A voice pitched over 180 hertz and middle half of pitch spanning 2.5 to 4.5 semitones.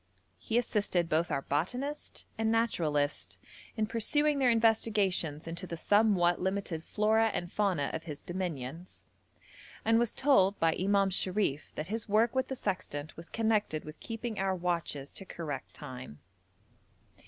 No: high, 190 Hz; wide, 5.5 semitones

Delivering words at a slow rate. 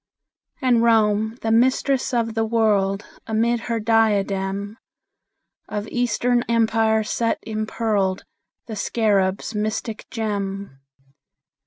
Yes: slow, 100 wpm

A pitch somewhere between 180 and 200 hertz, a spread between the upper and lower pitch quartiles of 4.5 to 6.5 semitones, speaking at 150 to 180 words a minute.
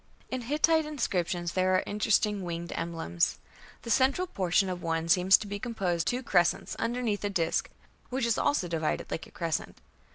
Yes: high, 190 Hz; wide, 5.6 semitones; average, 175 wpm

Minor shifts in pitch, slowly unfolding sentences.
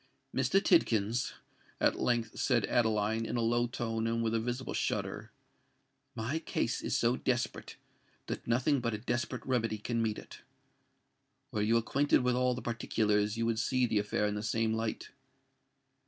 No: narrow, 1.6 semitones; average, 170 wpm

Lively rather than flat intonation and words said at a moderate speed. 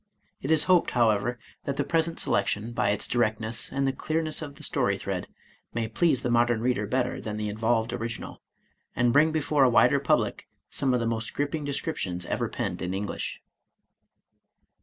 No: average, 4.4 semitones; average, 180 wpm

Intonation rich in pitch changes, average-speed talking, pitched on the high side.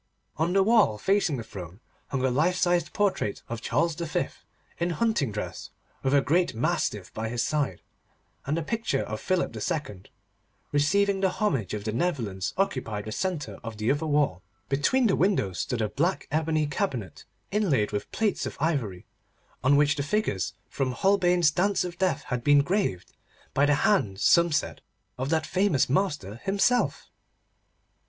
No: wide, 8.0 semitones; average, 165 wpm; medium, 145 Hz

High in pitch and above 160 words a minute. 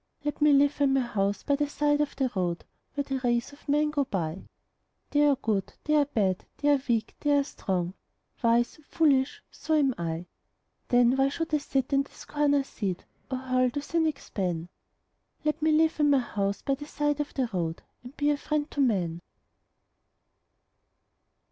Yes: very high, 275 Hz; average, 190 wpm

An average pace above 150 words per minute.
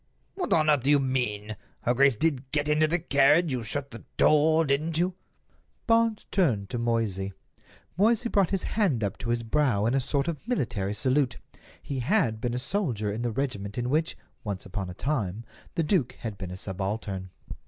Yes: average, 190 wpm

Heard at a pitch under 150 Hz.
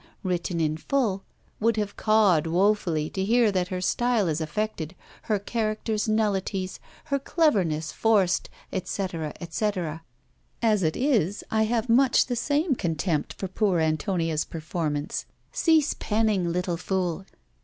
No: high, 195 Hz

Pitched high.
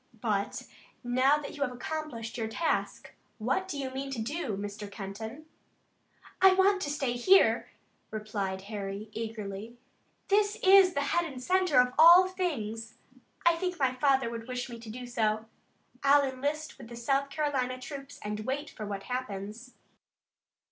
Yes: very high, 255 Hz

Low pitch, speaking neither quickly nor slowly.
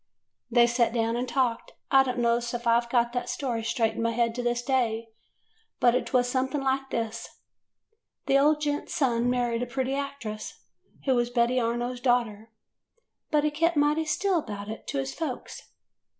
No: high, 245 Hz; average, 185 wpm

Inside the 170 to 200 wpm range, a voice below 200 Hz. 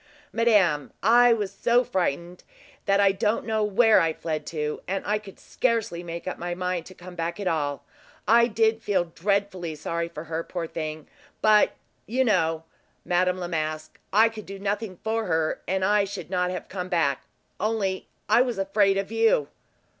Yes: average, 175 wpm; high, 190 Hz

